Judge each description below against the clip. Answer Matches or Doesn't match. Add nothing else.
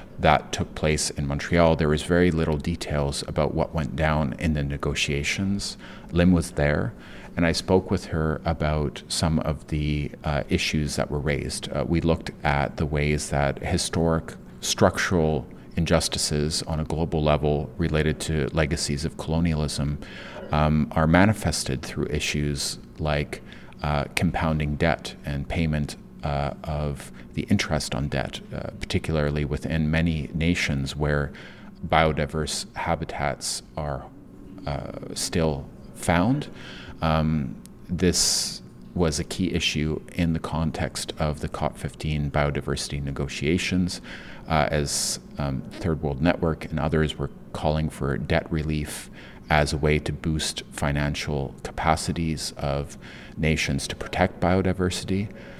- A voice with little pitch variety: Matches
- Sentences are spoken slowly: Matches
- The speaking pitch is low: Matches